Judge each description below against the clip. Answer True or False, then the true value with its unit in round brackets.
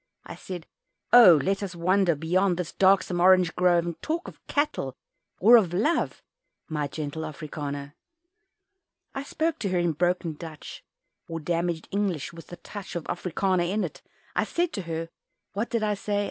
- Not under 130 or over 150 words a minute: False (170 wpm)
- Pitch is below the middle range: False (175 Hz)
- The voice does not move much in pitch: False (3.3 semitones)